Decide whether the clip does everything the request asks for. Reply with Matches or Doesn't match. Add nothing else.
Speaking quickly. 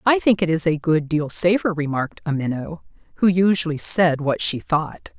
Doesn't match